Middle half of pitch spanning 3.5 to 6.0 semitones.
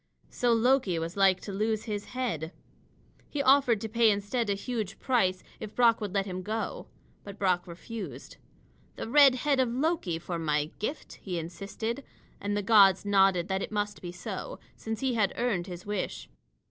Yes: average, 4.1 semitones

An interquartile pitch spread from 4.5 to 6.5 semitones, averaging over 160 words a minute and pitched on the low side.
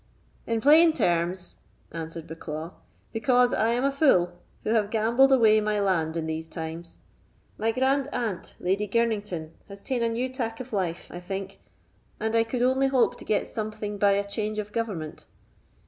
No: average, 4.9 semitones; average, 175 wpm; high, 215 Hz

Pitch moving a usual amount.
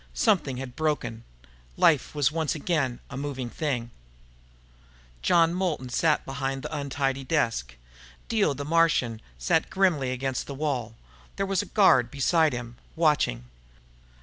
Yes: average, 4.2 semitones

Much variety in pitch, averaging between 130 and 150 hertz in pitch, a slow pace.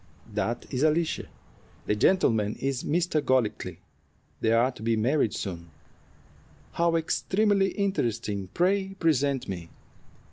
Yes: wide, 7.6 semitones; low, 135 Hz; slow, 115 wpm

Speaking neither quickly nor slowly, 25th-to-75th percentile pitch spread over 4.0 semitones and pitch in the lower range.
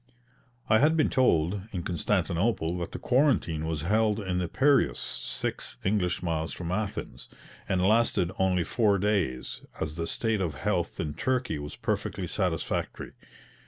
Yes: average, 150 wpm; average, 4.8 semitones; very low, 95 Hz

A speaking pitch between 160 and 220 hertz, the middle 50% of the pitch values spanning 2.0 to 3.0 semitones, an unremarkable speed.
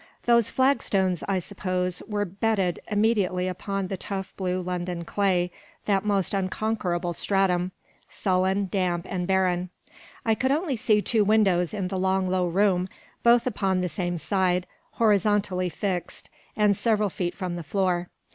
Yes: high, 190 Hz; narrow, 2.4 semitones; average, 150 wpm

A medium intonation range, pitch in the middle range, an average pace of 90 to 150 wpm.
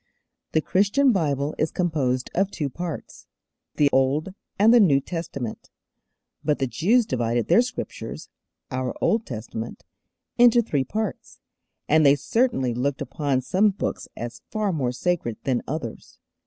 No: wide, 7.1 semitones; medium, 150 Hz; average, 140 wpm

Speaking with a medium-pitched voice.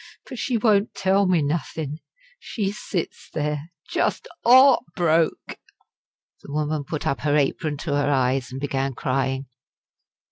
Yes: medium, 150 Hz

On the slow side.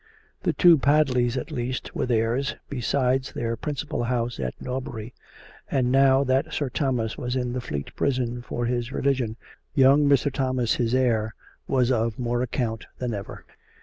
No: average, 160 wpm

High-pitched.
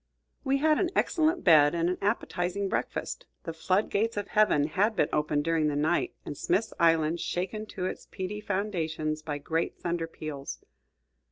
No: medium, 175 Hz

